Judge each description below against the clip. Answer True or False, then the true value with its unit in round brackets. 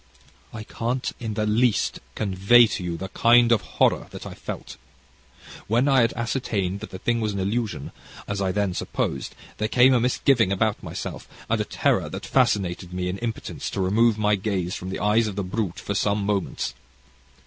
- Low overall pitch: True (105 Hz)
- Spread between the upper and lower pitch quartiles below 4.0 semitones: True (3.4 semitones)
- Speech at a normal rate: True (190 wpm)